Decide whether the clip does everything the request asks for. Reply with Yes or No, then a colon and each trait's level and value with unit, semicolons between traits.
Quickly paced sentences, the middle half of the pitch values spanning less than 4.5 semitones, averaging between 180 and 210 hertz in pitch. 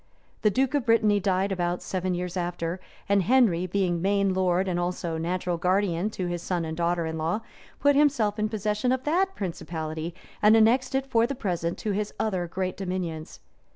No: average, 190 wpm; average, 3.8 semitones; medium, 185 Hz